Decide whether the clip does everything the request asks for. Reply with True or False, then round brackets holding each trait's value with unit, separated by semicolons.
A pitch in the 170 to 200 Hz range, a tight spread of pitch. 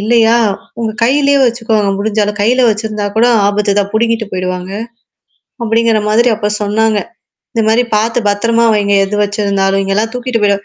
False (220 Hz; 2.2 semitones)